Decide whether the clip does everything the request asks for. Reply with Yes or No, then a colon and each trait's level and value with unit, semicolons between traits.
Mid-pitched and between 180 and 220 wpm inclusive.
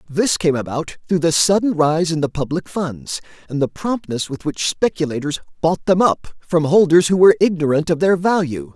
Yes: medium, 165 Hz; average, 190 wpm